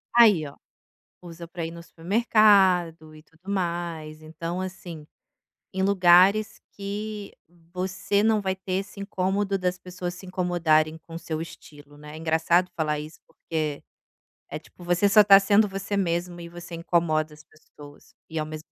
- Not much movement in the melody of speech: No, average, 3.3 semitones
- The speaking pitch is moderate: Yes, medium, 175 Hz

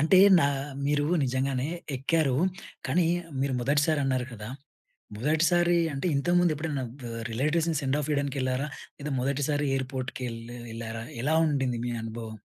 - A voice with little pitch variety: No, average, 3.0 semitones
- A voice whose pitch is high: No, medium, 140 Hz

